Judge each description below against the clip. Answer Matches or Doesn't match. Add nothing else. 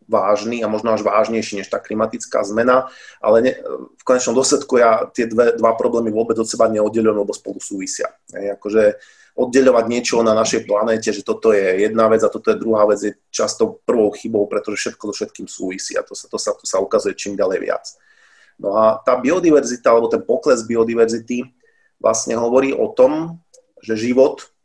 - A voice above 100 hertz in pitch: Matches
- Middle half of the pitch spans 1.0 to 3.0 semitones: Doesn't match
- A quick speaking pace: Matches